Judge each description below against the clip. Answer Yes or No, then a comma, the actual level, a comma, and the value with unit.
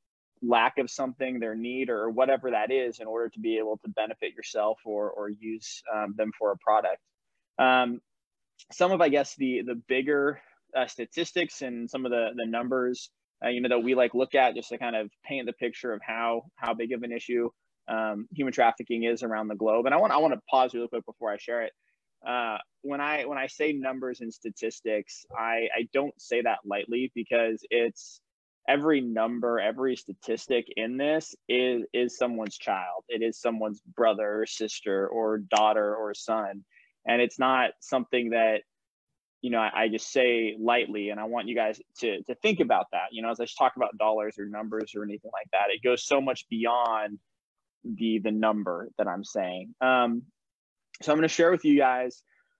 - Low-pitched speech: Yes, low, 115 Hz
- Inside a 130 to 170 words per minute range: No, average, 200 wpm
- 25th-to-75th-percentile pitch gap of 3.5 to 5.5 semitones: No, average, 2.8 semitones